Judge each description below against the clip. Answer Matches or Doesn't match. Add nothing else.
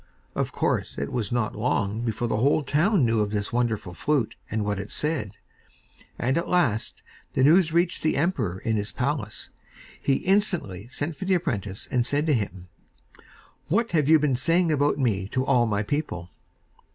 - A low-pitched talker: Matches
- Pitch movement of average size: Doesn't match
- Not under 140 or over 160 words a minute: Doesn't match